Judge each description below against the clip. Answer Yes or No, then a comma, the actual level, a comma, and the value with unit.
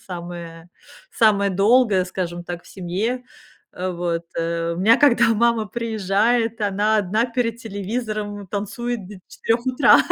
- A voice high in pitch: Yes, high, 205 Hz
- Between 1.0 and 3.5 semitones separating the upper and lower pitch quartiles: No, average, 4.2 semitones